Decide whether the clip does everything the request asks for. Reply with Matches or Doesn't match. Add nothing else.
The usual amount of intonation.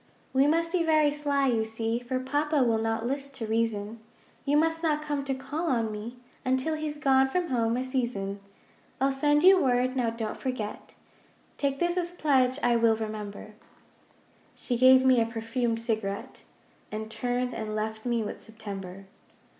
Matches